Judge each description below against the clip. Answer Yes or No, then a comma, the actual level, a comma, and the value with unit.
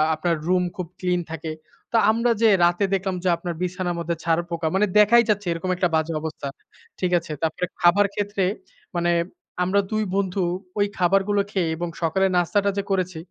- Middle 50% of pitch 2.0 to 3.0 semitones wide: Yes, average, 2.7 semitones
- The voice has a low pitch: No, medium, 180 Hz